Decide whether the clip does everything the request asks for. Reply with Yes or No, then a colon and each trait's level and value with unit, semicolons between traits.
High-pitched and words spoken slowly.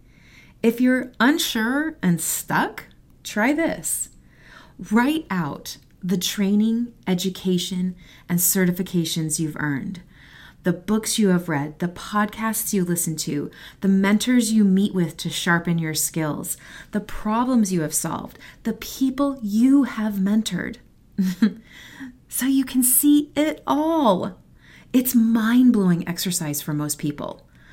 Yes: high, 200 Hz; slow, 125 wpm